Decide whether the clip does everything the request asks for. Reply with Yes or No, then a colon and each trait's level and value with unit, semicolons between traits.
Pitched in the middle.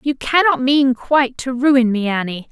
No: very high, 260 Hz